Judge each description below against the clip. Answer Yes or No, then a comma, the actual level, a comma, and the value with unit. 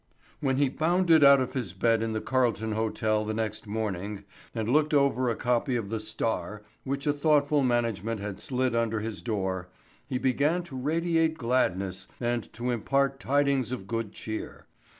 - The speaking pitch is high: No, low, 120 Hz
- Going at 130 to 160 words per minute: No, average, 170 wpm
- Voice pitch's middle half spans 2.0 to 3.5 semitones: No, average, 4.2 semitones